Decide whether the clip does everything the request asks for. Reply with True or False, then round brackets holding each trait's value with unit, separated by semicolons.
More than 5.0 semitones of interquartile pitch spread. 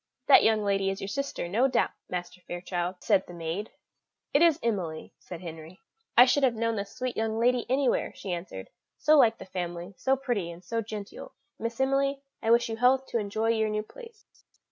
True (5.4 semitones)